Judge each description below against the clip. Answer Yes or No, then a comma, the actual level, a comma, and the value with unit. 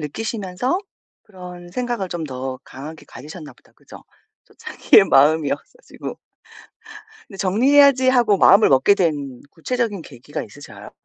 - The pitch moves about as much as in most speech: No, wide, 7.6 semitones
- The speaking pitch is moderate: Yes, medium, 180 Hz